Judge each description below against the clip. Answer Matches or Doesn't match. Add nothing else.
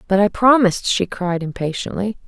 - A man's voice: Doesn't match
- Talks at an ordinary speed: Matches